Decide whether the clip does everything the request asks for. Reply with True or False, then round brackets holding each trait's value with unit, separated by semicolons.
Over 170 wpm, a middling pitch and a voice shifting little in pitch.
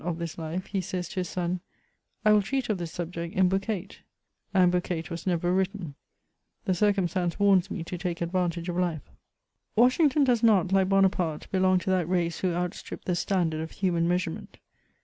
True (200 wpm; 180 Hz; 2.1 semitones)